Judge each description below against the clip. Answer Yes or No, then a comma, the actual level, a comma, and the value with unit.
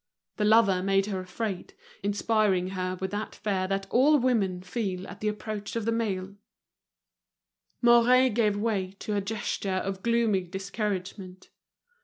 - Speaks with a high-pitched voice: Yes, high, 200 Hz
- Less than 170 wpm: Yes, average, 145 wpm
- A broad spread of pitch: No, average, 2.9 semitones